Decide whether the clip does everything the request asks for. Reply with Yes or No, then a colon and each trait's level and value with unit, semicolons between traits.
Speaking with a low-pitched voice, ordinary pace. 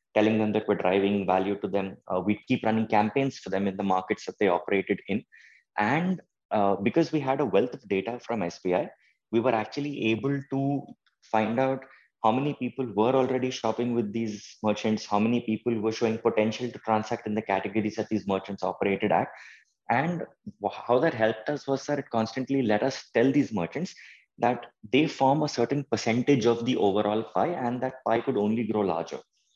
Yes: low, 115 Hz; average, 195 wpm